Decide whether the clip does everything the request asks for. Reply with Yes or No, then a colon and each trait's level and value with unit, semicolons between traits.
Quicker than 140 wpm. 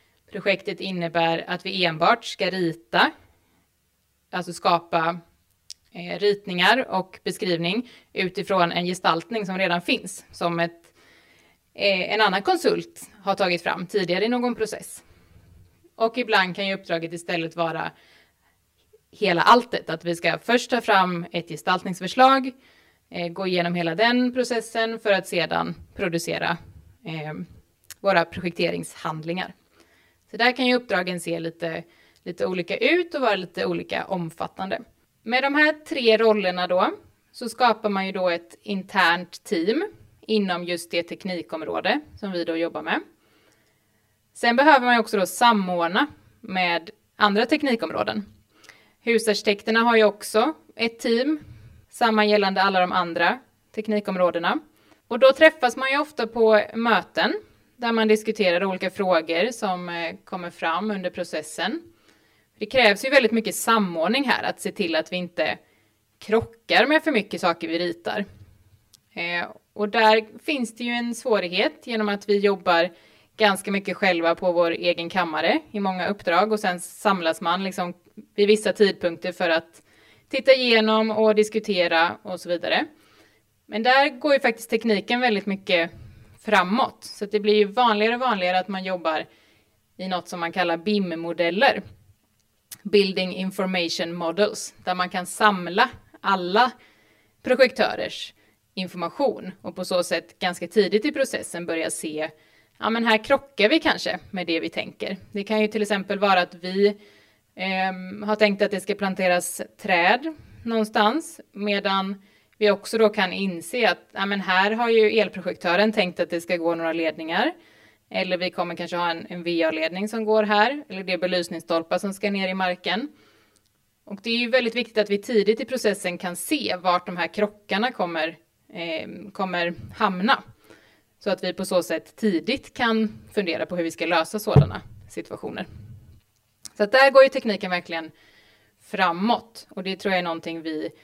Yes: average, 150 wpm